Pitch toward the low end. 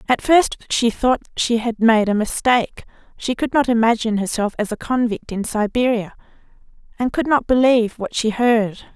No: high, 230 Hz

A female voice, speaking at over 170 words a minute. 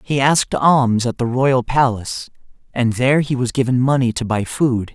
No: male; average, 195 wpm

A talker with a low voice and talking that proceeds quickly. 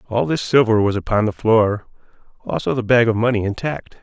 No: low, 115 Hz; average, 195 wpm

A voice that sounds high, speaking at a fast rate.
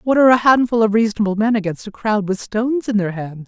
Yes: high, 215 Hz; fast, 260 wpm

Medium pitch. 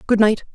No: high, 220 Hz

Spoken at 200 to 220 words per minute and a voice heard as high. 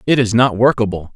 No: fast, 205 wpm; low, 115 Hz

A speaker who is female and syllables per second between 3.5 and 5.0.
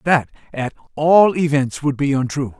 No: male; 4.5 syllables/s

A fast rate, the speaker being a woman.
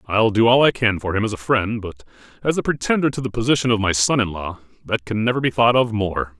No: fast, 270 wpm; male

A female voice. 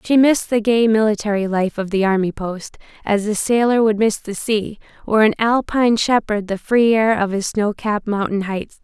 Yes: female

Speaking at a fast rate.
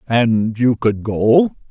No: average, 140 wpm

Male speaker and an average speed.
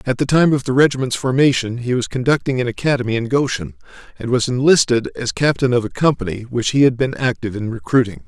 No: male; fast, 210 wpm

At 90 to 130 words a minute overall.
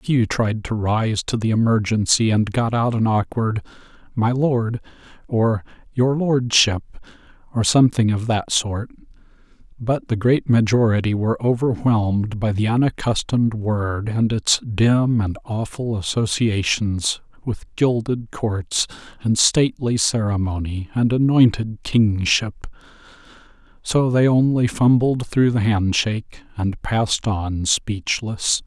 Yes: slow, 125 wpm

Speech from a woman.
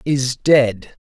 No: male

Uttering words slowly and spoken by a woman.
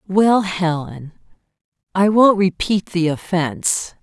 Yes: slow, 105 wpm; female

